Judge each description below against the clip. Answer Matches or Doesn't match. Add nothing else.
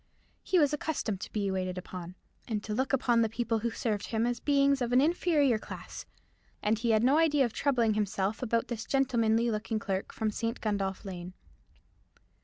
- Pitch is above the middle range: Matches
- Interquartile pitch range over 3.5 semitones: Matches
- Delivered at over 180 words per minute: Matches